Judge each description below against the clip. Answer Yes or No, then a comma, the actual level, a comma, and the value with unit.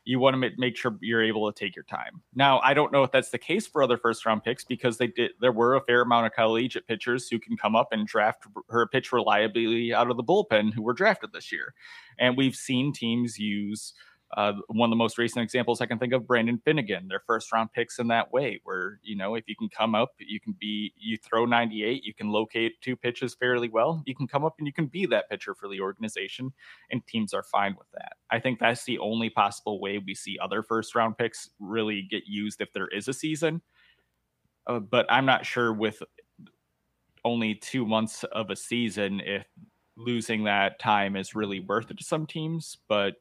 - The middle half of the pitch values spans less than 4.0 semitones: Yes, average, 2.7 semitones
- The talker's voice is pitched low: Yes, low, 115 Hz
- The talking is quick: Yes, fast, 225 wpm